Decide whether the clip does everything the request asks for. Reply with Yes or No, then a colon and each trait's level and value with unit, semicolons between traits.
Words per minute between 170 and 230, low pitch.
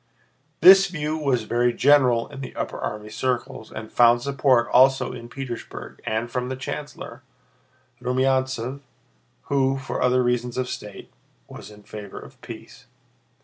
No: average, 145 wpm; low, 125 Hz